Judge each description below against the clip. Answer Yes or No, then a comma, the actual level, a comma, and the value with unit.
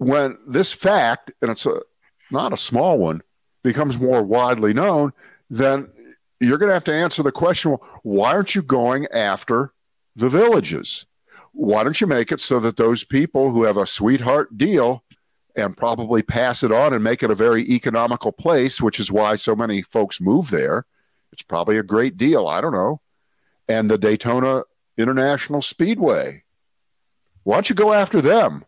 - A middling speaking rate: Yes, average, 175 wpm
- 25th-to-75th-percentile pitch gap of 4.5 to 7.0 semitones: Yes, average, 4.8 semitones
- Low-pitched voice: Yes, low, 125 Hz